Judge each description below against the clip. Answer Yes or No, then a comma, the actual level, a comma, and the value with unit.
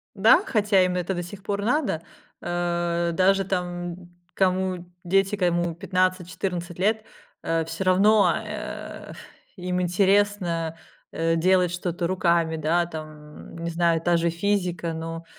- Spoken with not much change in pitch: Yes, narrow, 2.1 semitones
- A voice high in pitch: No, medium, 175 Hz